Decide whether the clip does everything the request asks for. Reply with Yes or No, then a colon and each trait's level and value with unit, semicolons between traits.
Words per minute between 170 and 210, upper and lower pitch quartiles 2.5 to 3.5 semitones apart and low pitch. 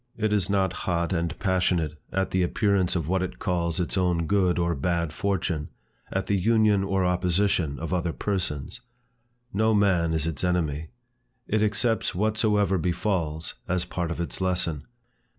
No: average, 160 wpm; average, 2.8 semitones; very low, 90 Hz